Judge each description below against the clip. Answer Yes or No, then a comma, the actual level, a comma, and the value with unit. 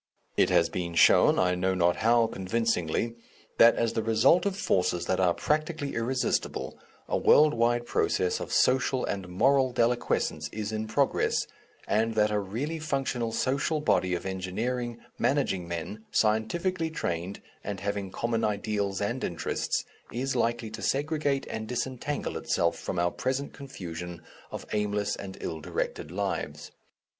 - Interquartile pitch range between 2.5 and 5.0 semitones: No, wide, 5.5 semitones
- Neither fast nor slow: Yes, average, 150 wpm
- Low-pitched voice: Yes, low, 110 Hz